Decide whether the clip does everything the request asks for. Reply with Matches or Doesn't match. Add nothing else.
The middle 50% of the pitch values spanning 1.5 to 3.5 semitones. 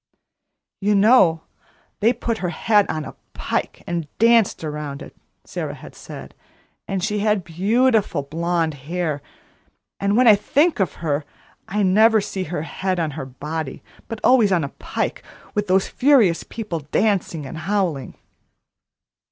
Doesn't match